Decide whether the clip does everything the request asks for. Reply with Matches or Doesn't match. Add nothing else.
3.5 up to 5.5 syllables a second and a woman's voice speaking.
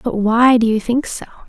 Matches